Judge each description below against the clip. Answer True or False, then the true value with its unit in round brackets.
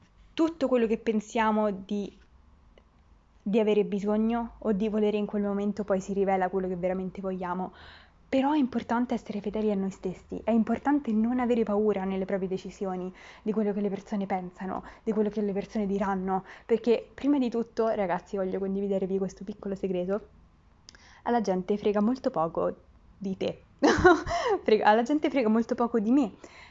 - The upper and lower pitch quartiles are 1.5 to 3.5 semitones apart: True (3.1 semitones)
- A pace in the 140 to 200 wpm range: True (165 wpm)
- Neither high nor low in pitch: False (210 Hz)